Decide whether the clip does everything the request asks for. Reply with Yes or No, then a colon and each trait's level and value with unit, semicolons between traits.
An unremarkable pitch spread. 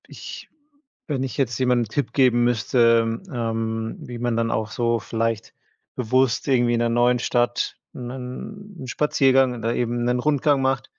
No: narrow, 2.1 semitones